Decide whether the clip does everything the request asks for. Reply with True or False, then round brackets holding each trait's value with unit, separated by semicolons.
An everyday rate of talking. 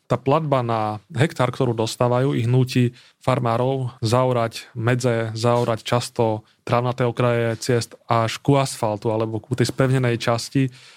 True (130 wpm)